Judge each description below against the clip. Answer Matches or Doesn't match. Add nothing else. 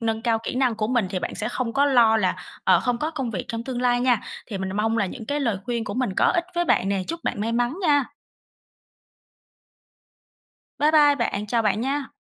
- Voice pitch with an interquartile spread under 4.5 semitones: Matches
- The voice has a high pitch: Matches